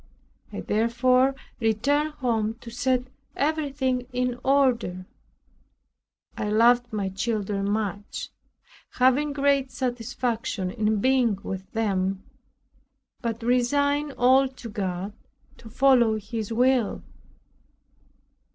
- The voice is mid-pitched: No, high, 240 Hz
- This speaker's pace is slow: Yes, slow, 95 wpm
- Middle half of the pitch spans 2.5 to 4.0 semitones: Yes, average, 3.6 semitones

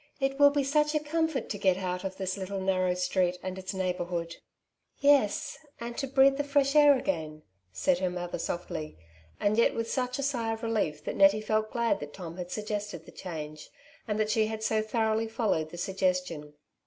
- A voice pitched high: Yes, high, 205 Hz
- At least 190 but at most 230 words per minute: Yes, fast, 205 wpm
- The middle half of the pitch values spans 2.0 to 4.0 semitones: No, average, 4.9 semitones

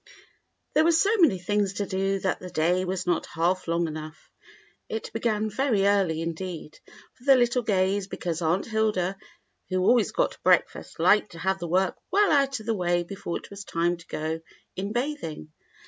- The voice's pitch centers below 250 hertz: Yes, high, 190 Hz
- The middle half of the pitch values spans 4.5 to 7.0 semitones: No, average, 4.0 semitones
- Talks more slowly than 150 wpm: No, average, 185 wpm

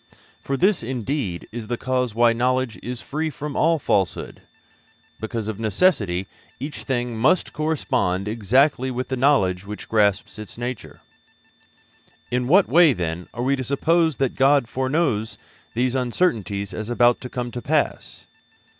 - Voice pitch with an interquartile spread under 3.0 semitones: No, average, 4.1 semitones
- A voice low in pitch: Yes, low, 125 Hz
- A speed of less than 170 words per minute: Yes, average, 145 wpm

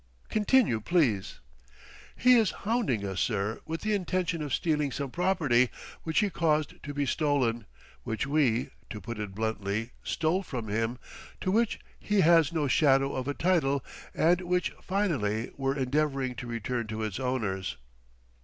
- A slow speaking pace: No, average, 155 wpm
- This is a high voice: No, medium, 140 Hz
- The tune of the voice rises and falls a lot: Yes, wide, 6.9 semitones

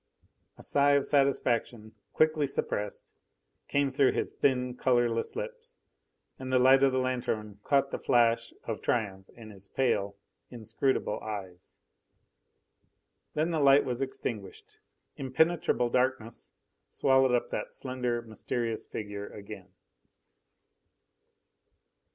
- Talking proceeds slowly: Yes, slow, 115 wpm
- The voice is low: Yes, low, 125 Hz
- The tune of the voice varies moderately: Yes, average, 3.6 semitones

